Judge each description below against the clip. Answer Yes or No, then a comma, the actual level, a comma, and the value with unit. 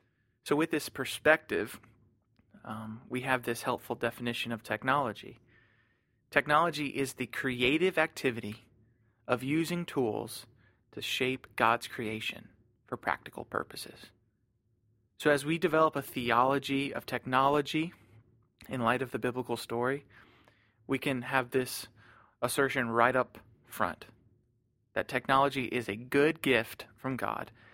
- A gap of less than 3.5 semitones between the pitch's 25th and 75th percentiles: Yes, average, 2.9 semitones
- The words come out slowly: Yes, slow, 125 wpm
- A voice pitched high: No, low, 120 Hz